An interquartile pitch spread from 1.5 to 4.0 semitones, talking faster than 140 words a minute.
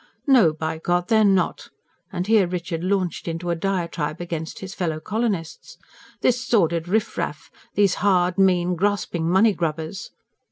Yes: average, 3.2 semitones; average, 155 wpm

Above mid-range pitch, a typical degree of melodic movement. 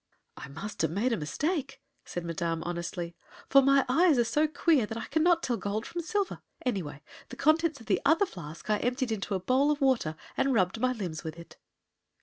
No: high, 235 Hz; wide, 8.5 semitones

